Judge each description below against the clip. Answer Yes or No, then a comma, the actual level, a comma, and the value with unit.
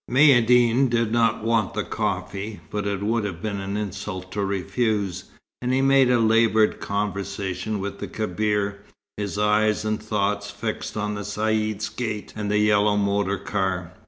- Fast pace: No, average, 160 wpm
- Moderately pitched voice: No, low, 105 Hz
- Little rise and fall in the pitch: Yes, narrow, 1.8 semitones